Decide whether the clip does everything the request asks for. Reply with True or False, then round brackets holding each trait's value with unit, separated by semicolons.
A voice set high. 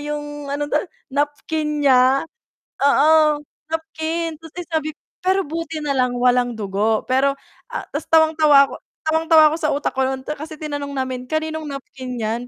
True (295 Hz)